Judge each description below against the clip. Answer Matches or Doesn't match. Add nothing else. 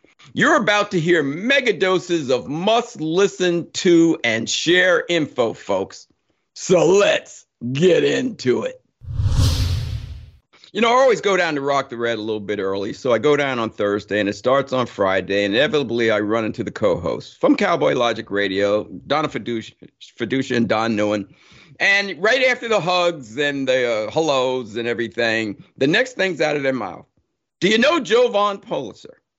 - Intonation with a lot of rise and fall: Matches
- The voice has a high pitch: Doesn't match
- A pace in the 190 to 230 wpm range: Doesn't match